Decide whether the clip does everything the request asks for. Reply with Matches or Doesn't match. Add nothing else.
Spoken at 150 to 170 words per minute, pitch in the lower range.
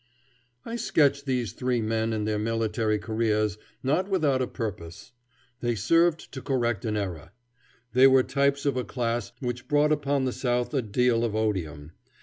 Matches